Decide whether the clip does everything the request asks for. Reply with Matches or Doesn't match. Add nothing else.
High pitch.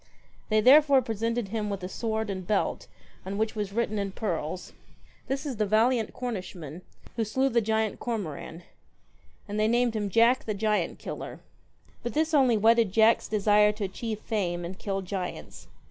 Matches